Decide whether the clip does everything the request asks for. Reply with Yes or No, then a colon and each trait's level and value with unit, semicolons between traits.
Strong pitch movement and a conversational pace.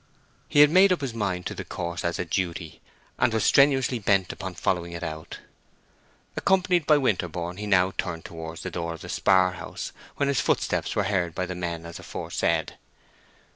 Yes: wide, 6.2 semitones; average, 190 wpm